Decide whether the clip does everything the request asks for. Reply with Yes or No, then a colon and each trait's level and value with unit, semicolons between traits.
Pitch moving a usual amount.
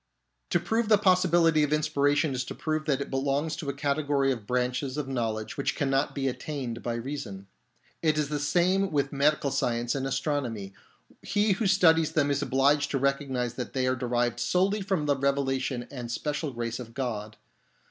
Yes: average, 3.4 semitones